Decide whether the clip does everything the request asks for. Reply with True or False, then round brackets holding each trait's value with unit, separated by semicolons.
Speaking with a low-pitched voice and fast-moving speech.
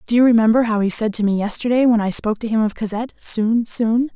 False (225 Hz; 260 wpm)